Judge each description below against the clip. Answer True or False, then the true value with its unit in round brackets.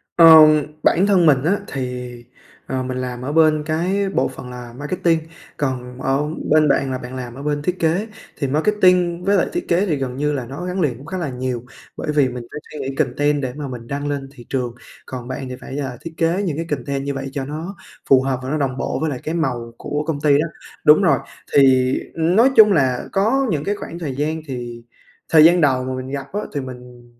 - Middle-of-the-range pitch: True (145 Hz)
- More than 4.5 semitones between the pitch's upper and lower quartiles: False (4.2 semitones)